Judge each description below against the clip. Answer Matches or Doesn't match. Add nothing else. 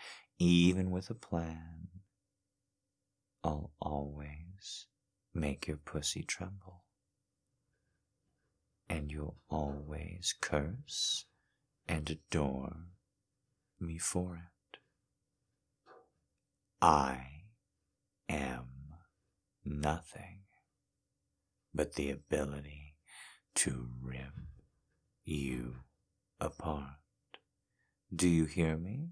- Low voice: Matches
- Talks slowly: Matches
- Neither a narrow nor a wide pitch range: Matches